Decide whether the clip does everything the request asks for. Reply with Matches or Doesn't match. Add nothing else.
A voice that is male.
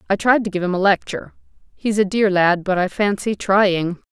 Doesn't match